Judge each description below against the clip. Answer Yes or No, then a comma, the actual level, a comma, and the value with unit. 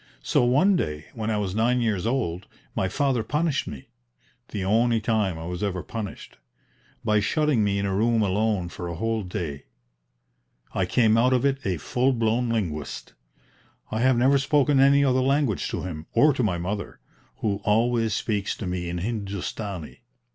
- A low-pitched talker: Yes, low, 110 Hz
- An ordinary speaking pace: Yes, average, 175 wpm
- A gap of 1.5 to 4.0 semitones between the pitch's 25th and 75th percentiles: No, average, 4.7 semitones